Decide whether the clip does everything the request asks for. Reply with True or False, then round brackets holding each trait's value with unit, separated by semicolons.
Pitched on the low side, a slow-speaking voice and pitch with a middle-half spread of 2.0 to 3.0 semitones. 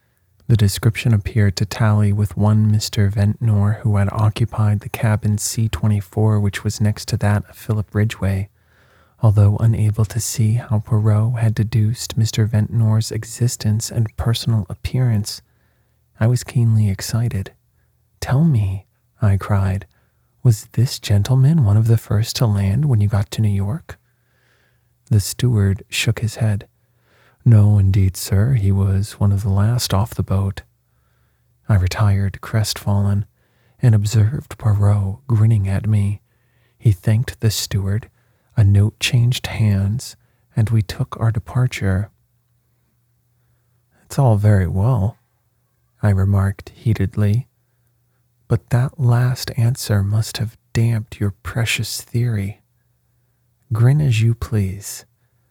True (110 Hz; 130 wpm; 2.7 semitones)